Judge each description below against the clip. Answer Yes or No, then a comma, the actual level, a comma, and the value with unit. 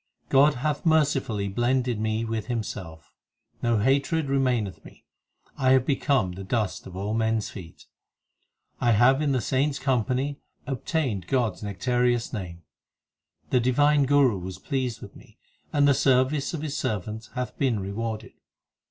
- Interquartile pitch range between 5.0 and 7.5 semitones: No, average, 4.2 semitones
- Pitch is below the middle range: Yes, low, 125 Hz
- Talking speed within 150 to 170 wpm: Yes, average, 160 wpm